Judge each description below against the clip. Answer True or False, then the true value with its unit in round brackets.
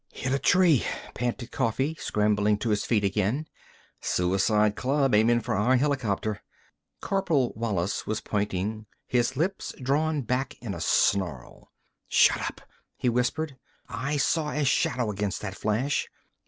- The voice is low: True (120 Hz)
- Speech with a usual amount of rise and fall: True (4.7 semitones)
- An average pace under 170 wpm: True (140 wpm)